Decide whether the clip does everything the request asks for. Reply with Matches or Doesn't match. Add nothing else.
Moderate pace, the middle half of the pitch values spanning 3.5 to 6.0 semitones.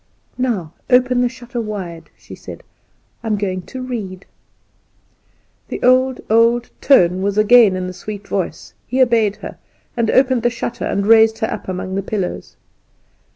Matches